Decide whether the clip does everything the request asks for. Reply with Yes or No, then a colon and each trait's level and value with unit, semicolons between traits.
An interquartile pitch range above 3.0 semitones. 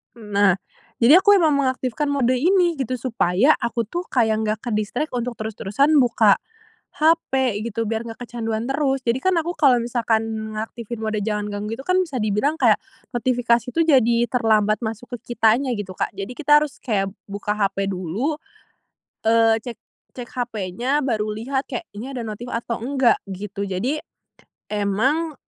Yes: average, 3.9 semitones